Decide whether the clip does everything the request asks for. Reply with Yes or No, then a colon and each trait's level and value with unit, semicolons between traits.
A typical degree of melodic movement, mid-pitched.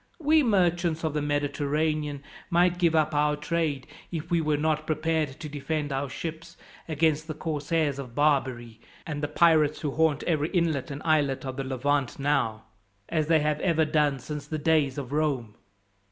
No: narrow, 2.2 semitones; medium, 150 Hz